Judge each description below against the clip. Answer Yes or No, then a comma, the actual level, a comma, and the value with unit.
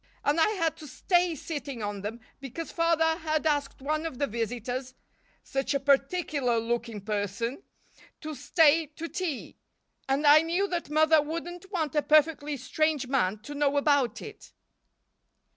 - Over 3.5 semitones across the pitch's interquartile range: Yes, average, 4.2 semitones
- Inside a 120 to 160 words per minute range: Yes, average, 155 wpm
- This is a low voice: No, very high, 290 Hz